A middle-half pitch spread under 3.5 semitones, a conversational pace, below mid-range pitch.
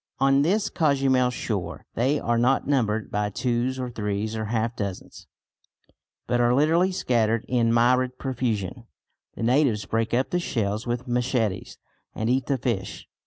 Yes: average, 3.0 semitones; average, 155 wpm; low, 120 Hz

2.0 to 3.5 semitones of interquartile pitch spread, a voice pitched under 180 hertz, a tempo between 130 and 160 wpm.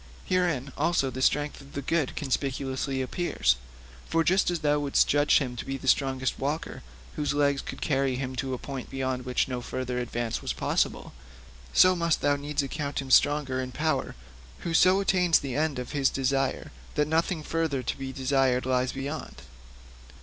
No: narrow, 2.5 semitones; medium, 140 Hz; average, 180 wpm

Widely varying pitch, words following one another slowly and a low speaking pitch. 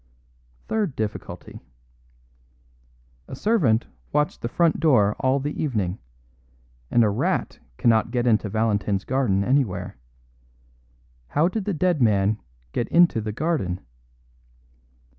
Yes: wide, 6.2 semitones; slow, 115 wpm; low, 120 Hz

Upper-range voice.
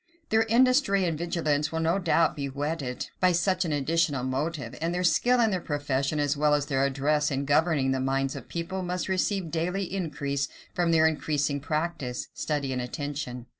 No: medium, 155 Hz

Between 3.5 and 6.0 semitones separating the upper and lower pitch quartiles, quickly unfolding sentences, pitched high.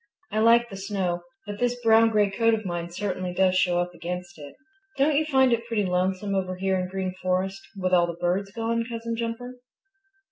Yes: average, 3.9 semitones; fast, 210 wpm; high, 195 Hz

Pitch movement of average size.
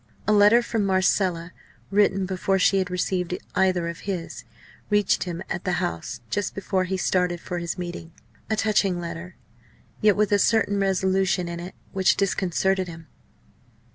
No: narrow, 2.1 semitones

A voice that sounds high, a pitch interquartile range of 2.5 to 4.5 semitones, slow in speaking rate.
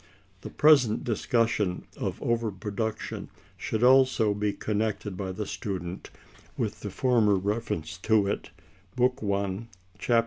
No: low, 105 Hz; average, 2.9 semitones; slow, 130 wpm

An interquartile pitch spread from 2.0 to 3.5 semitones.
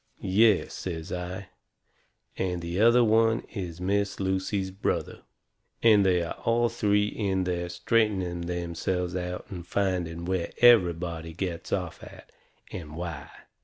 Yes: average, 2.7 semitones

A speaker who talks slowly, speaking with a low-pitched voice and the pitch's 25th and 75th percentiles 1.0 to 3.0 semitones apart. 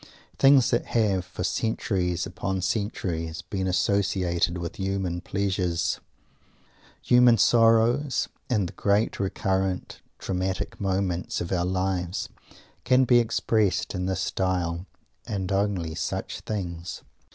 Yes: slow, 115 wpm; very low, 95 Hz; average, 2.7 semitones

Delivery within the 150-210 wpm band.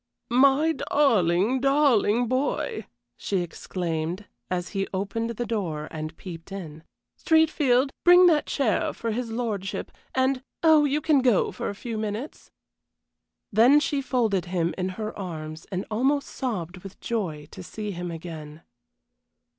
No: average, 140 wpm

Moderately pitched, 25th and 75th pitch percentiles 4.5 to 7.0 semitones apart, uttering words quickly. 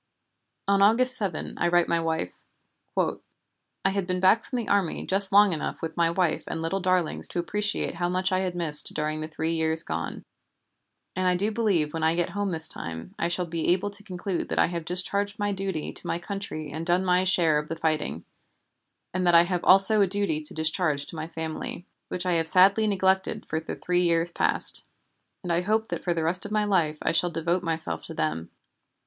No: medium, 175 Hz; average, 3.1 semitones; fast, 215 wpm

